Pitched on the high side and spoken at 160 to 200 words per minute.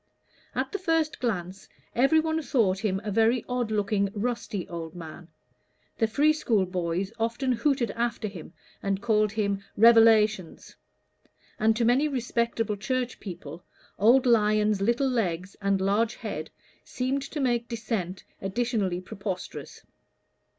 No: high, 220 Hz; slow, 135 wpm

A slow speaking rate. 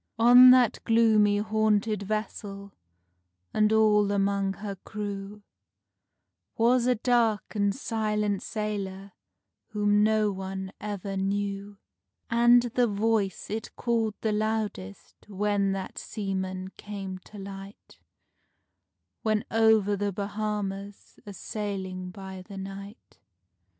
Yes: slow, 110 wpm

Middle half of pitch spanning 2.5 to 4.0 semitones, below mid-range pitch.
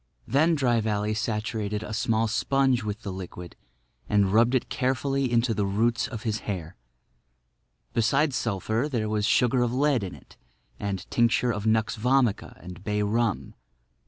Yes: average, 3.0 semitones; low, 110 Hz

